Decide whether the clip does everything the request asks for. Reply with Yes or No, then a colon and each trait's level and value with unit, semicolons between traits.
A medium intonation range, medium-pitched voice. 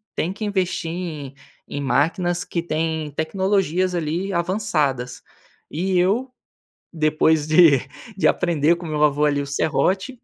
Yes: average, 3.6 semitones; medium, 165 Hz